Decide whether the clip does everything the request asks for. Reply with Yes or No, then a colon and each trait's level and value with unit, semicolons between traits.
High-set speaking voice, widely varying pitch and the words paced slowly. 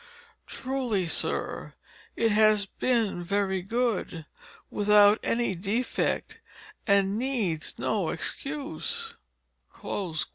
No: high, 210 Hz; average, 4.0 semitones; slow, 80 wpm